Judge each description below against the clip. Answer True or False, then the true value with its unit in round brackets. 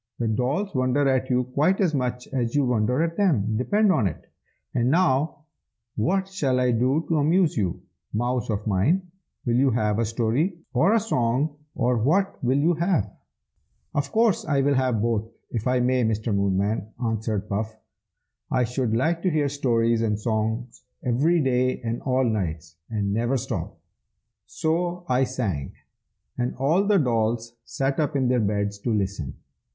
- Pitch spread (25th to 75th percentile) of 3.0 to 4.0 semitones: False (4.7 semitones)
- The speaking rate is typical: True (170 wpm)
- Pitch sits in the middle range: False (125 Hz)